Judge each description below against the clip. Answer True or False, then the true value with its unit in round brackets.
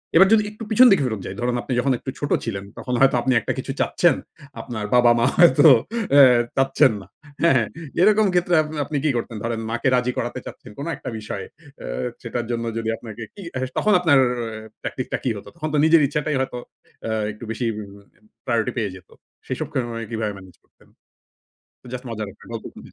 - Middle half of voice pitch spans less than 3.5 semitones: False (5.0 semitones)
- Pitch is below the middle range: True (125 Hz)